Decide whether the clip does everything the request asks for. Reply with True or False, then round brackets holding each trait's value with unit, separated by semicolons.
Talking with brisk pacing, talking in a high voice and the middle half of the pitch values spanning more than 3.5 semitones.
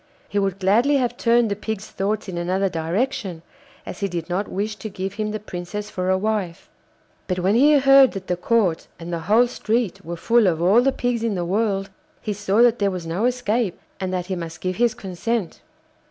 True (215 wpm; 200 Hz; 4.0 semitones)